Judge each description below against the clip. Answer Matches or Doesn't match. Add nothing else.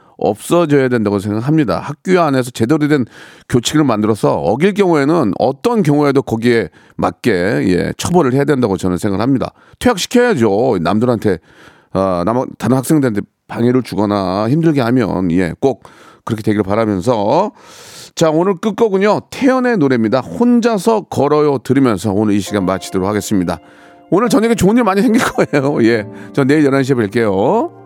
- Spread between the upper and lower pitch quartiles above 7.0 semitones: Matches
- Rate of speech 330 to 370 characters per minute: Matches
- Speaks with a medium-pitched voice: Doesn't match